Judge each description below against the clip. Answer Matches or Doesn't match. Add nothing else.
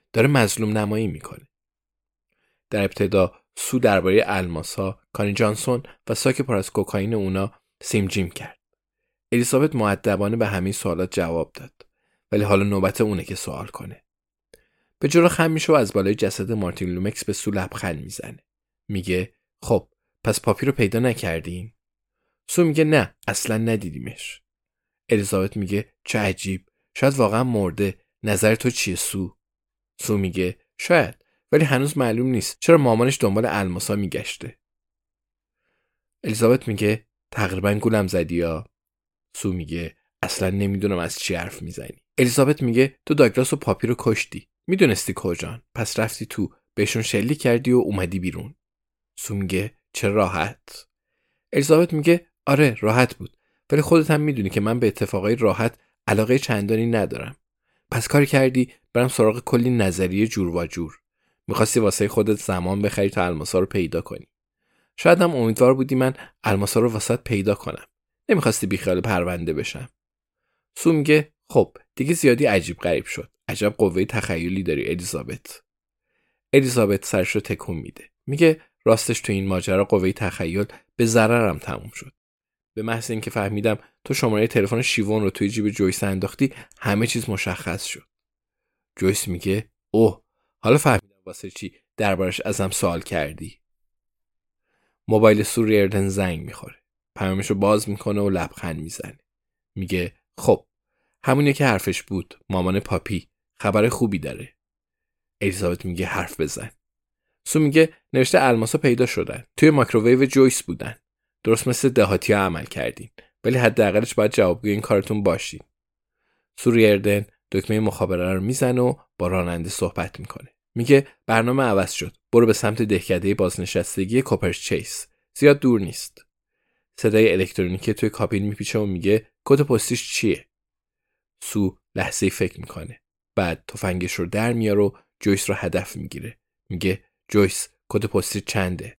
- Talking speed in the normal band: Matches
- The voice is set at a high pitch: Doesn't match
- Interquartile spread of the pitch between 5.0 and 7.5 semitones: Doesn't match